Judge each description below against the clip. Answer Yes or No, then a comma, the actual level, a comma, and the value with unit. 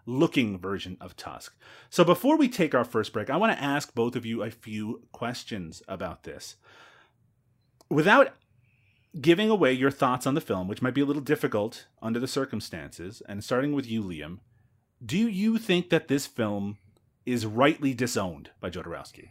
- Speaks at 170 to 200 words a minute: Yes, average, 175 wpm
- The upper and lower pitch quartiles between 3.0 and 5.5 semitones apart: Yes, average, 4.8 semitones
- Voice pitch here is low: Yes, low, 125 Hz